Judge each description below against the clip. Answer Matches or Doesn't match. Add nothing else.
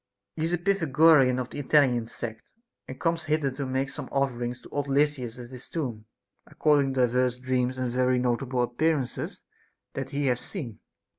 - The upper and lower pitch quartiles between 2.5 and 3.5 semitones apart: Matches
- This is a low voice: Matches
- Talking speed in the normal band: Matches